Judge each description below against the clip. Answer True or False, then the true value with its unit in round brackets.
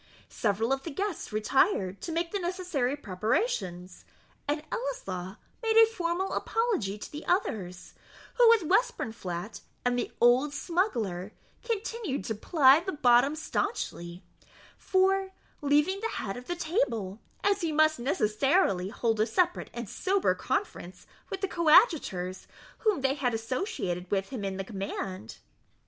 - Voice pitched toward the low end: False (280 Hz)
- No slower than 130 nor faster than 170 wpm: True (140 wpm)